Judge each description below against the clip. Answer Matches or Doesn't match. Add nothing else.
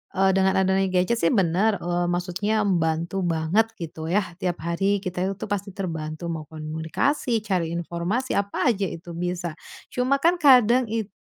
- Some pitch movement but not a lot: Matches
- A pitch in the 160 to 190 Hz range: Matches